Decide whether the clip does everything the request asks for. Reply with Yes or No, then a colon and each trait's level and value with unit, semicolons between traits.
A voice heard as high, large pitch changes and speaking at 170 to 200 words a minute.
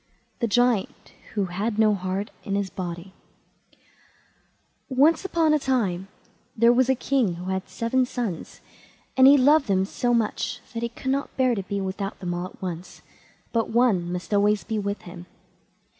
No: high, 210 Hz; average, 4.9 semitones; average, 175 wpm